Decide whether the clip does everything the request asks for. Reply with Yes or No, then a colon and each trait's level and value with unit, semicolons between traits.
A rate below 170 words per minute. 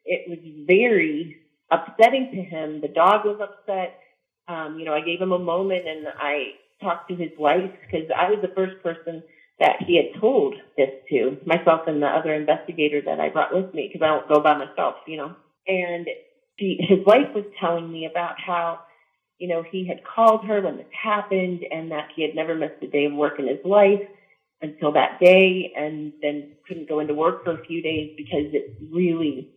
No: fast, 205 wpm